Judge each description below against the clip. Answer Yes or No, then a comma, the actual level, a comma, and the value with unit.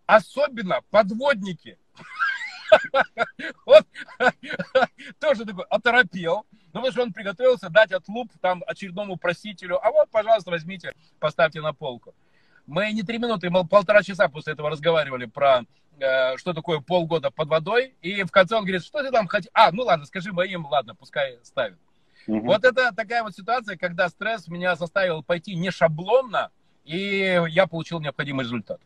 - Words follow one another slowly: No, average, 150 wpm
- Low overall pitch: No, high, 190 Hz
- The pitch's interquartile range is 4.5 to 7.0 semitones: Yes, wide, 5.6 semitones